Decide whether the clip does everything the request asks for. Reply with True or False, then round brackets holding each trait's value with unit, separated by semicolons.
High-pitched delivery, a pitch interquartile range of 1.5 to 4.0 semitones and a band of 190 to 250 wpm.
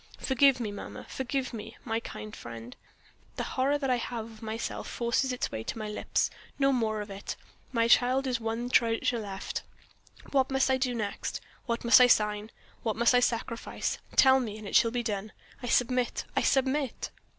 True (235 Hz; 3.0 semitones; 195 wpm)